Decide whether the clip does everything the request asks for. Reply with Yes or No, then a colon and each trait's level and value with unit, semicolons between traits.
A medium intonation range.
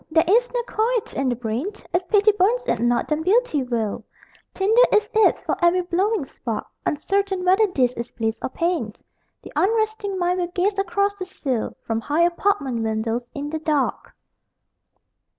No: wide, 7.8 semitones